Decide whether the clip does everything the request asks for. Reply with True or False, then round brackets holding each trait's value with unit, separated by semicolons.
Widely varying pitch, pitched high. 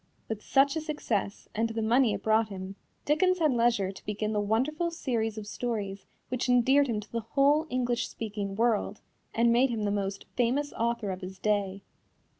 False (3.7 semitones; 225 Hz)